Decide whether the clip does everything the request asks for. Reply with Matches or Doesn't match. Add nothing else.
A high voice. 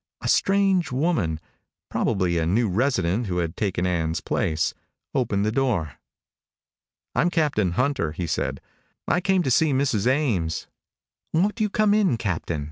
Doesn't match